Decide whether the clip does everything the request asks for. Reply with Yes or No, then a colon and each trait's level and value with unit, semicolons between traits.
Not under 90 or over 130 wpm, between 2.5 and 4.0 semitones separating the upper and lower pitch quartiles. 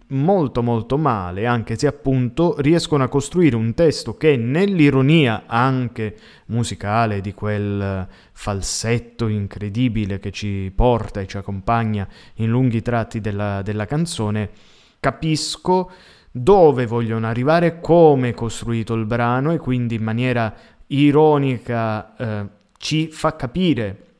No: average, 120 wpm; average, 5.0 semitones